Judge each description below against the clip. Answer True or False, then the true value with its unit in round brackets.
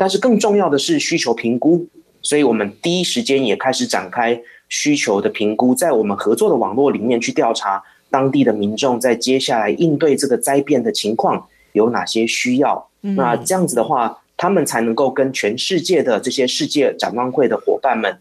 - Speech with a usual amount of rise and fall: False (8.2 semitones)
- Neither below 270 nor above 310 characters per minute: True (305 characters per minute)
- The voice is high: False (140 Hz)